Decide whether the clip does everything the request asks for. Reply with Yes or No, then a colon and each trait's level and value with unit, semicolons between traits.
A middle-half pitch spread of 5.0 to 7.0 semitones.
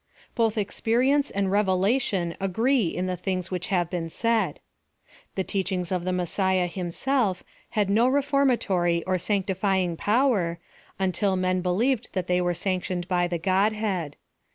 No: average, 3.2 semitones